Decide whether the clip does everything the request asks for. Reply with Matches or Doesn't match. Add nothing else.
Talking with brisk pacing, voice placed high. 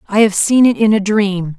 Matches